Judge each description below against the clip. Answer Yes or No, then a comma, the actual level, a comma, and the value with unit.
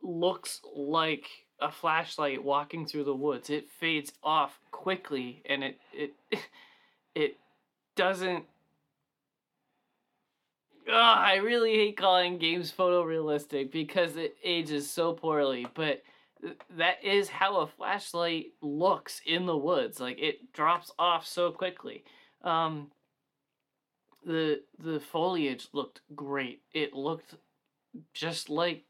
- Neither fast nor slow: No, slow, 115 wpm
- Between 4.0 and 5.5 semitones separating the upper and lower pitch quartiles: No, average, 3.5 semitones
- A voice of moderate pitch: Yes, medium, 165 Hz